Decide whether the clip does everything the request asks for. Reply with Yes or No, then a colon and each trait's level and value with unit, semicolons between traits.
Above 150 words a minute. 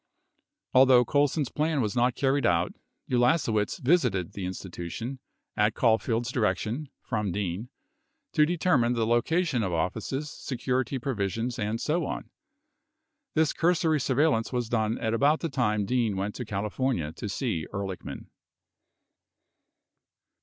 No: average, 140 wpm